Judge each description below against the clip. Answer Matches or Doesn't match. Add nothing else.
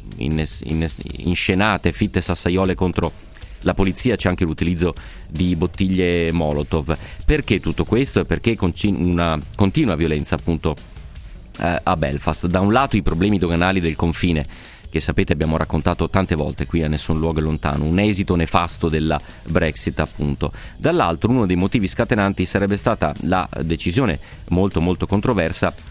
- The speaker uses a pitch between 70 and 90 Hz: Matches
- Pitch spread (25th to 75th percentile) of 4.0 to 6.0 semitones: Doesn't match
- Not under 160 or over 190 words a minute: Doesn't match